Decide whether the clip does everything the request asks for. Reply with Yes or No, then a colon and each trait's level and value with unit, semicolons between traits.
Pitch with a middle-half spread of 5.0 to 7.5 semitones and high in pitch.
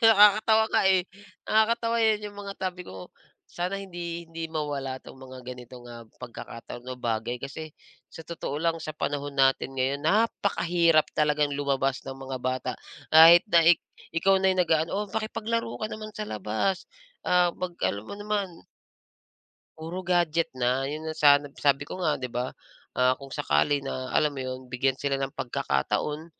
No: wide, 5.6 semitones; medium, 155 Hz